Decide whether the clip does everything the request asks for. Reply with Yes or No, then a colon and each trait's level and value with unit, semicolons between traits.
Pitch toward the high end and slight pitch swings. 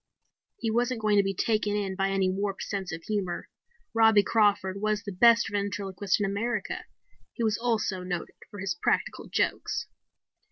Yes: high, 205 Hz; narrow, 2.1 semitones